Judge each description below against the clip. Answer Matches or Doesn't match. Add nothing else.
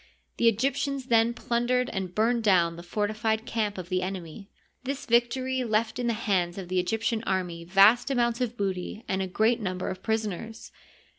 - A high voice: Matches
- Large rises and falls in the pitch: Doesn't match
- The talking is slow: Doesn't match